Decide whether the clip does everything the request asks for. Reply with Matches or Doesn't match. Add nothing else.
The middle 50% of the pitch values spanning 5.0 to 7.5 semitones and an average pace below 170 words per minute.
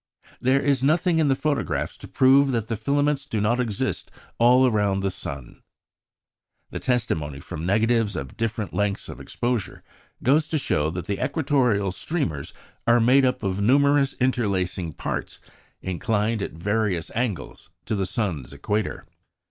Matches